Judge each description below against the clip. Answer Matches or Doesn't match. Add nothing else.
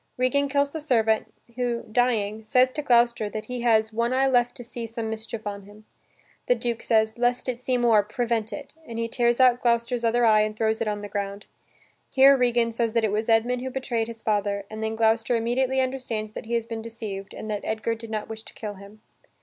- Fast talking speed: Matches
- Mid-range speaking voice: Doesn't match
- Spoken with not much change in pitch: Matches